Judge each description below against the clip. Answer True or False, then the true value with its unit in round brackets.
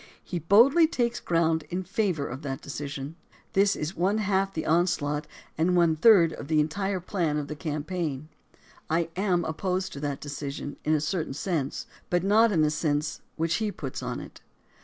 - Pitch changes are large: False (4.1 semitones)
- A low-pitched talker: False (165 Hz)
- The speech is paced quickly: False (180 wpm)